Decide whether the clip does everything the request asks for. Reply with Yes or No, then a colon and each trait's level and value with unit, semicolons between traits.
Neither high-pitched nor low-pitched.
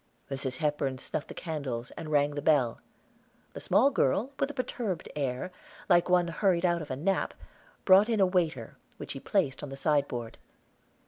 Yes: medium, 155 Hz